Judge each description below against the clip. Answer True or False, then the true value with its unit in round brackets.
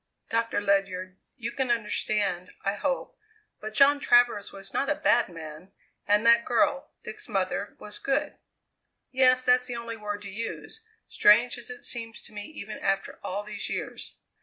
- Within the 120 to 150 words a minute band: False (165 wpm)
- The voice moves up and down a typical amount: True (3.7 semitones)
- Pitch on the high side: True (215 Hz)